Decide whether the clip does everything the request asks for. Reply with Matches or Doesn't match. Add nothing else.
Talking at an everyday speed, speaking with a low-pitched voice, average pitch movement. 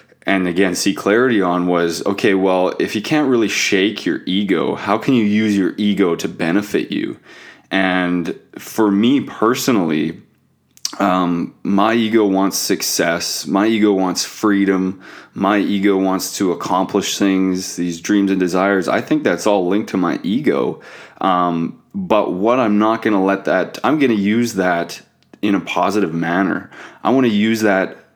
Doesn't match